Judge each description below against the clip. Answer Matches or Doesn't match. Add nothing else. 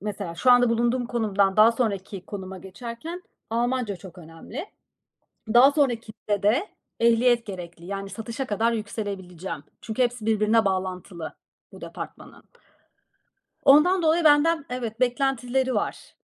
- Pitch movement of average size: Matches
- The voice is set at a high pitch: Matches